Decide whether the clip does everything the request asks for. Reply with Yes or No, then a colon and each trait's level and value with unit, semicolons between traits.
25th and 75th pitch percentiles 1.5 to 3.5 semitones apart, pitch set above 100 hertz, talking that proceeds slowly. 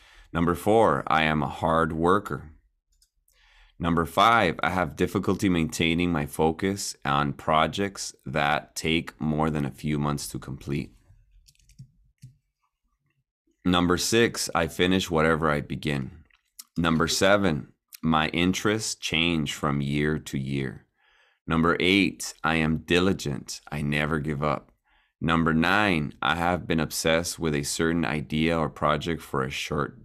No: average, 3.1 semitones; very low, 80 Hz; slow, 130 wpm